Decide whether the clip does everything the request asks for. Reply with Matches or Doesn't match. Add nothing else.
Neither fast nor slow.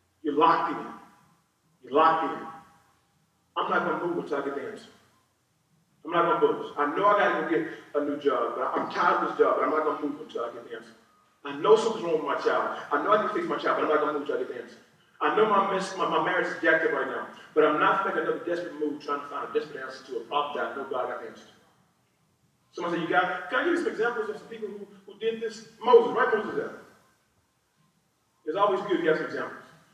Doesn't match